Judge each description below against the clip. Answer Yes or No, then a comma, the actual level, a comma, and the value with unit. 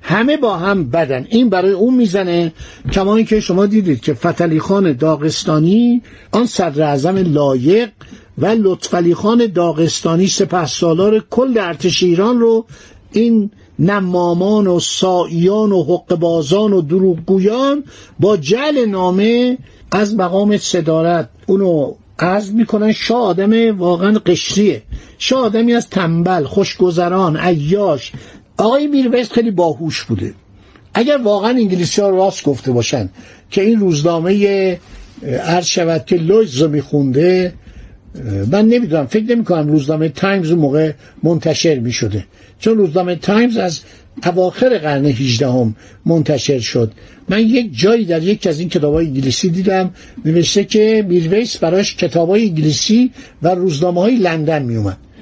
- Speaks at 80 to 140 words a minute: Yes, average, 130 wpm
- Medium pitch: Yes, medium, 180 Hz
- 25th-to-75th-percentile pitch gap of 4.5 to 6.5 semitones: Yes, average, 4.9 semitones